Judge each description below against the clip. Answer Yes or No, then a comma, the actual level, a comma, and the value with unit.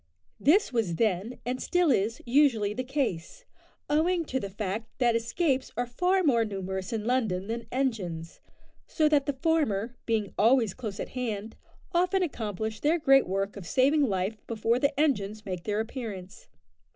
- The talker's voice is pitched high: Yes, high, 230 Hz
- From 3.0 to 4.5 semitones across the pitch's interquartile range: No, wide, 5.4 semitones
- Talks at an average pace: Yes, average, 165 wpm